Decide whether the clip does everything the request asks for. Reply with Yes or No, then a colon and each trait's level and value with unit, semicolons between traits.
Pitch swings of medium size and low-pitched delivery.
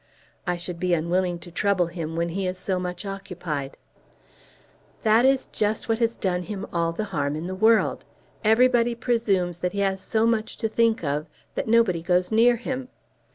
No: average, 4.3 semitones; high, 190 Hz